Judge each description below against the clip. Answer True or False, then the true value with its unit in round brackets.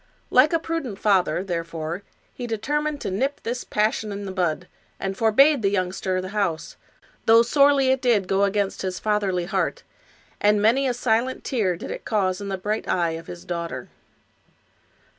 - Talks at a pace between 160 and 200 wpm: True (175 wpm)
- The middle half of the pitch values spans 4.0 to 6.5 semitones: True (4.7 semitones)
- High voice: True (205 Hz)